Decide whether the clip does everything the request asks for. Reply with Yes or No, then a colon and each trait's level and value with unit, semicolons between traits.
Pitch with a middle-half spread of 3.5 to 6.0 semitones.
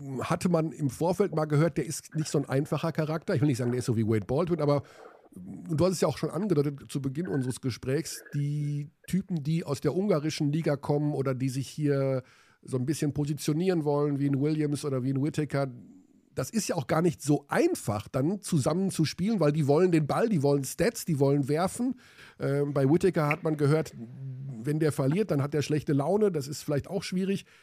No: average, 3.0 semitones